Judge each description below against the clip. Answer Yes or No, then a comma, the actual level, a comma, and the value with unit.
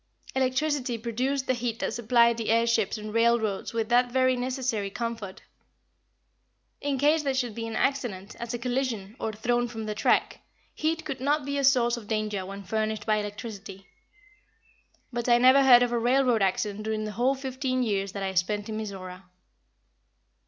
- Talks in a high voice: Yes, high, 235 Hz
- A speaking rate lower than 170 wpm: No, average, 180 wpm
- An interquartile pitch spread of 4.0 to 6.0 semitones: No, average, 3.2 semitones